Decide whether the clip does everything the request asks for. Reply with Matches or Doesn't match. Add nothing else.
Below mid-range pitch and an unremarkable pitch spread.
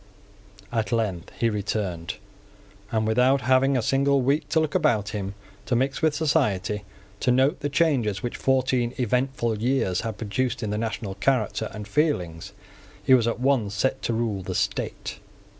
Matches